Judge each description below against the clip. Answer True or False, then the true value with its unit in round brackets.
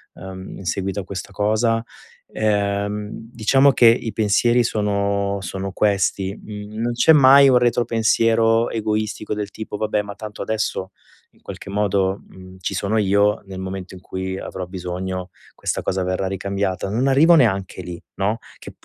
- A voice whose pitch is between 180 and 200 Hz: False (100 Hz)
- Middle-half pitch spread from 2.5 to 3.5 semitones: True (2.8 semitones)